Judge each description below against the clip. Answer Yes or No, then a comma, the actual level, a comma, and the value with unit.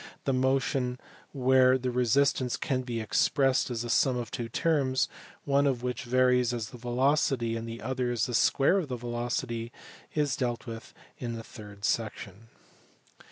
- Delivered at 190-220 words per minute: No, average, 165 wpm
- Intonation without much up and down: Yes, narrow, 2.0 semitones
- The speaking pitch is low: Yes, low, 125 Hz